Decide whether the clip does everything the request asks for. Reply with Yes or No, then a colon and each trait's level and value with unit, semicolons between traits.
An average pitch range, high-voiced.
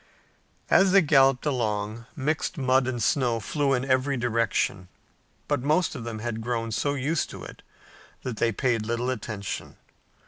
No: average, 3.5 semitones; low, 125 Hz